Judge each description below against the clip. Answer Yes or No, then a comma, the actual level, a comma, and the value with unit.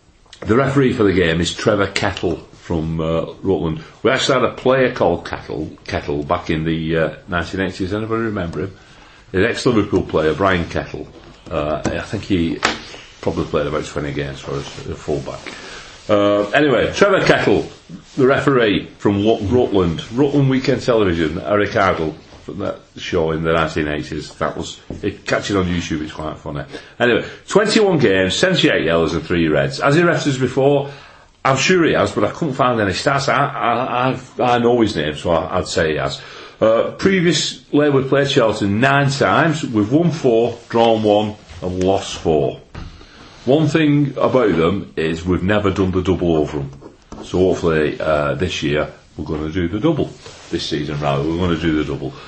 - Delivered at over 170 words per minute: Yes, average, 180 wpm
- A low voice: Yes, very low, 95 Hz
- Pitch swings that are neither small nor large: No, wide, 6.5 semitones